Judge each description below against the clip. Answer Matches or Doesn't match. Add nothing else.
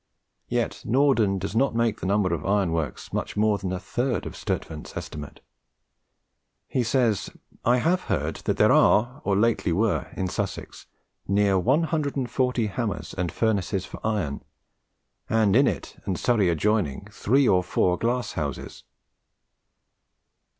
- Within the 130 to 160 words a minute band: Matches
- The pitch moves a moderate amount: Matches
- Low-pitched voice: Matches